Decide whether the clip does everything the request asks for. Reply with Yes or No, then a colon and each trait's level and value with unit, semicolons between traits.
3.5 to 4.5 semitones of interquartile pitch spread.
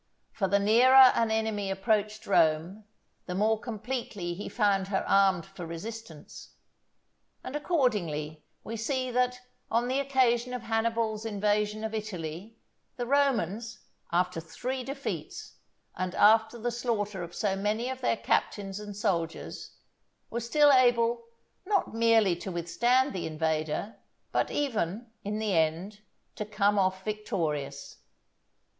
Yes: average, 3.9 semitones